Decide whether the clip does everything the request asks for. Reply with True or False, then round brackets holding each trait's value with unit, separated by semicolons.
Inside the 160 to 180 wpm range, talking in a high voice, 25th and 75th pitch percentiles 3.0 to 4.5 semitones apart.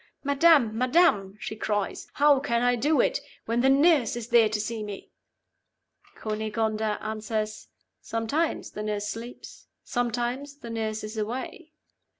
False (140 wpm; 230 Hz; 3.7 semitones)